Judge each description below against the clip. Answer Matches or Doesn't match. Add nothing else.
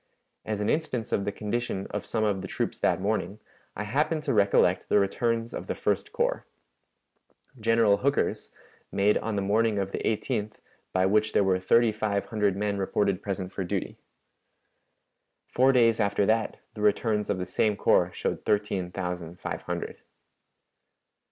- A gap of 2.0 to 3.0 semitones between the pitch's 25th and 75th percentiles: Matches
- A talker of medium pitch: Doesn't match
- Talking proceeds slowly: Doesn't match